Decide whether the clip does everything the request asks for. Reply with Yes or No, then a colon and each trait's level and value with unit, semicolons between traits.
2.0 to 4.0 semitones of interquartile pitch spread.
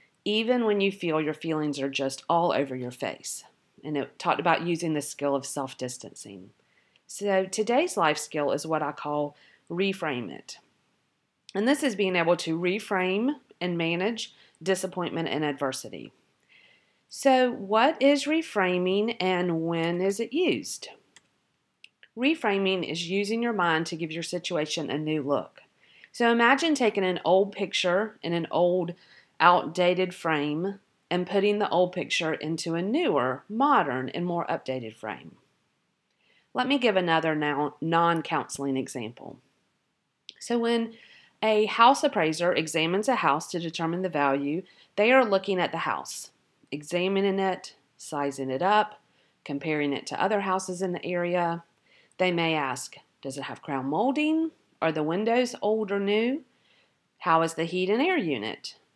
No: average, 4.8 semitones